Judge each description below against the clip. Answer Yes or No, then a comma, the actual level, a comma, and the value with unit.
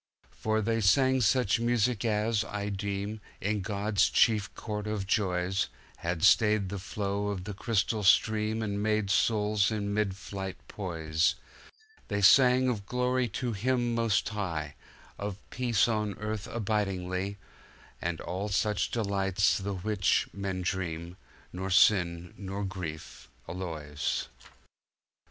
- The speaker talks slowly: Yes, slow, 125 wpm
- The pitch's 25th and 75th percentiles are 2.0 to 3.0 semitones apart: Yes, narrow, 2.4 semitones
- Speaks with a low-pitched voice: Yes, low, 100 Hz